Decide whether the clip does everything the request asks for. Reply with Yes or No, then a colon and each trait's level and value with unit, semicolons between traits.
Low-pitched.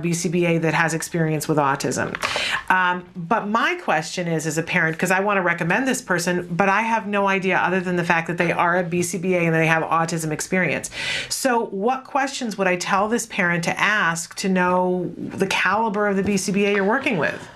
No: medium, 180 Hz